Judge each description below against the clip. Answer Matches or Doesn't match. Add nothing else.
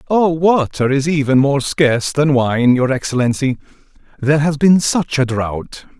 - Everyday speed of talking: Matches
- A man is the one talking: Matches